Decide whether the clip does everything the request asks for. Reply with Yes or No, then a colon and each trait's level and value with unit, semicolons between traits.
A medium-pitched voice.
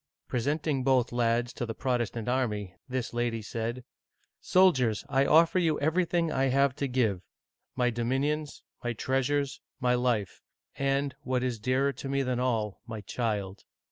No: low, 125 Hz